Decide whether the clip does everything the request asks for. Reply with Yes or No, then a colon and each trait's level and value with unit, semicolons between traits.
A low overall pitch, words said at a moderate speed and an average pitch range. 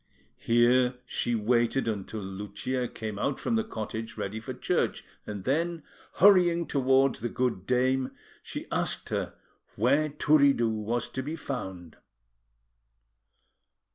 No: low, 125 Hz; slow, 125 wpm; average, 4.2 semitones